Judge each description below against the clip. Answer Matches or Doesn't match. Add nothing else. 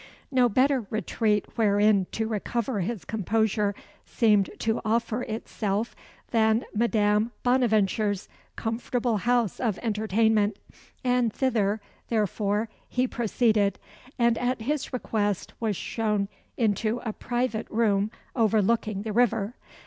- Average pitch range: Doesn't match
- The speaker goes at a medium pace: Doesn't match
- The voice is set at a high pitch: Matches